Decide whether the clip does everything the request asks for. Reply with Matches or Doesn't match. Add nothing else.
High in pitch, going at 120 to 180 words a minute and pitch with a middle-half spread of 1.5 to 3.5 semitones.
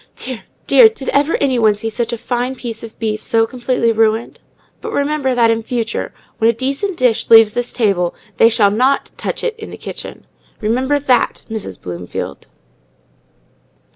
Matches